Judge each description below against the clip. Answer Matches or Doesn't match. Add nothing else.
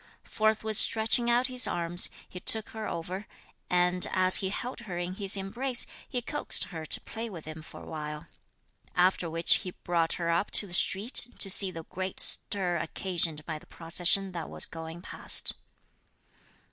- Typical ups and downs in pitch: Matches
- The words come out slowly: Doesn't match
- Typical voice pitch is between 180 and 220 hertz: Matches